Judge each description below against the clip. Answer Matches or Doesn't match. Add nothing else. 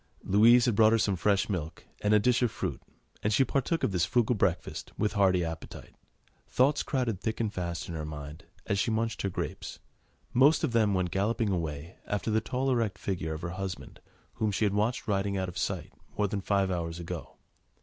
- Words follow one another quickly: Matches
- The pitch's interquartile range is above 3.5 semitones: Matches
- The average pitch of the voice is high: Doesn't match